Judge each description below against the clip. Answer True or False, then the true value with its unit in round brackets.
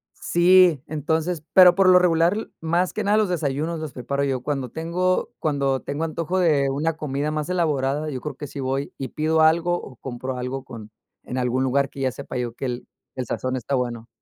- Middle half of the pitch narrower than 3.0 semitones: False (3.9 semitones)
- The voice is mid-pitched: True (145 Hz)